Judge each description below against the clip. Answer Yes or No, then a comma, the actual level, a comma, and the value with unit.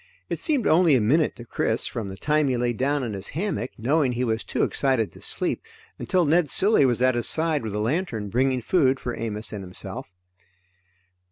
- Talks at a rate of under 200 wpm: No, fast, 205 wpm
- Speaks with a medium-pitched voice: No, low, 130 Hz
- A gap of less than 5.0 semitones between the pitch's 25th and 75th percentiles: No, wide, 5.4 semitones